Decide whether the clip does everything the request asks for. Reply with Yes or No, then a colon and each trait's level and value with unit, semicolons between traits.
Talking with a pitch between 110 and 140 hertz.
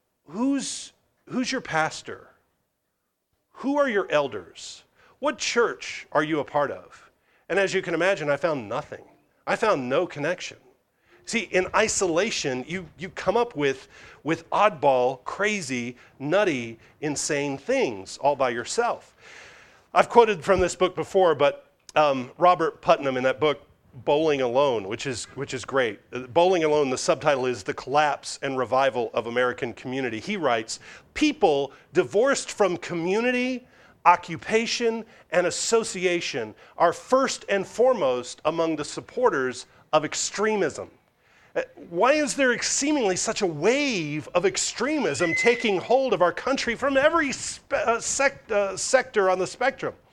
No: medium, 180 Hz